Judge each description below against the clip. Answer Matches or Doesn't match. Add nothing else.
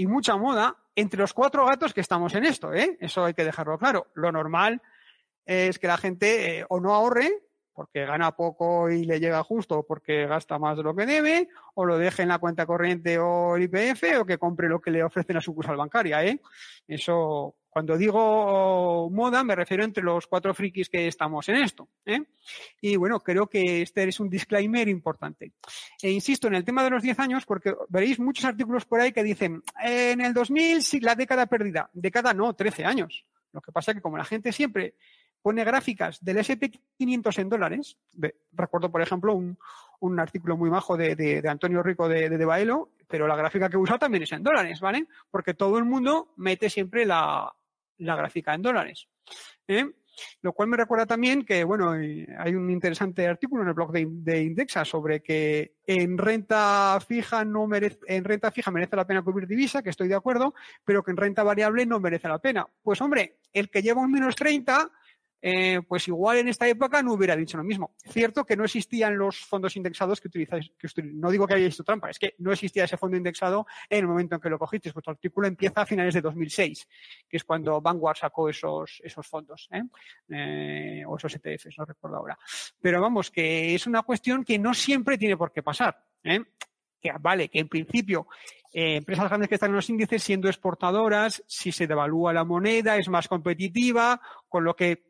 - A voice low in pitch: Doesn't match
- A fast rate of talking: Matches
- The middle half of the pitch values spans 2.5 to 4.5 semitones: Doesn't match